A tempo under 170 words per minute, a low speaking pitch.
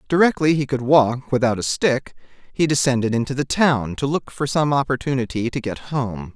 No: average, 190 wpm; low, 130 Hz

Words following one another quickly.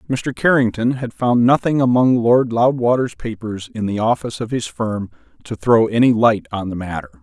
No: average, 185 wpm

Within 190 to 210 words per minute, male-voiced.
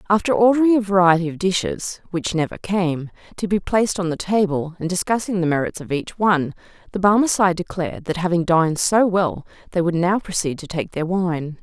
No: average, 195 wpm; female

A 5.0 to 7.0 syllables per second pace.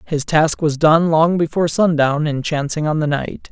No: 4.7 syllables/s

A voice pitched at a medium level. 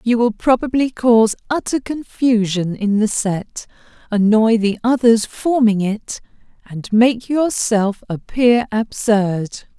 No: high, 225 Hz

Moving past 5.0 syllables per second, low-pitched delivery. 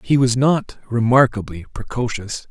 No: 4.5 syllables/s; low, 120 Hz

